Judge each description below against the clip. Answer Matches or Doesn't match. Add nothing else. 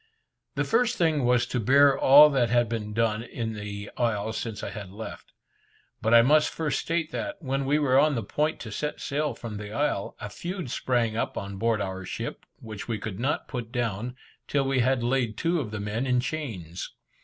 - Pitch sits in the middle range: Doesn't match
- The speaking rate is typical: Doesn't match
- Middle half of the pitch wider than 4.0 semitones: Matches